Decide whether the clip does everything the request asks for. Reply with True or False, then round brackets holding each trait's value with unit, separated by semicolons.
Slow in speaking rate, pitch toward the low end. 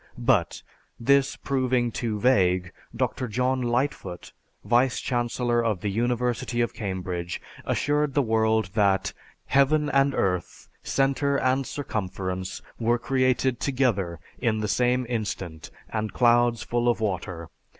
True (125 wpm; 120 Hz)